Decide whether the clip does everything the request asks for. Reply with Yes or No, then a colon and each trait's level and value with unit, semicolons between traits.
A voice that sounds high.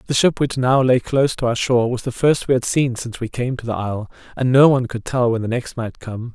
No: low, 125 Hz